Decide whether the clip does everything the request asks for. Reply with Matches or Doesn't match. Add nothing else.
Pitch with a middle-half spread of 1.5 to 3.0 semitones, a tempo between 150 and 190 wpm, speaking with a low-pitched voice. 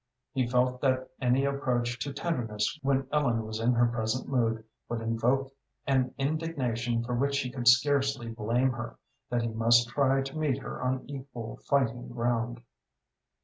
Matches